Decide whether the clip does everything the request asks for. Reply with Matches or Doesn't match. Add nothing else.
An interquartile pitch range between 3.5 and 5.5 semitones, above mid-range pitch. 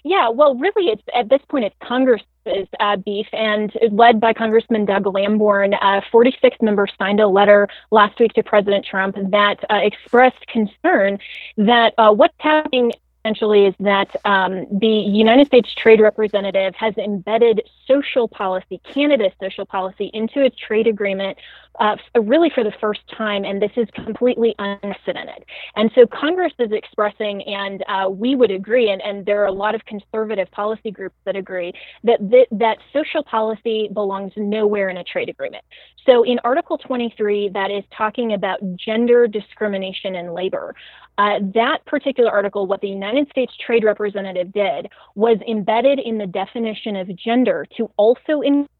Doesn't match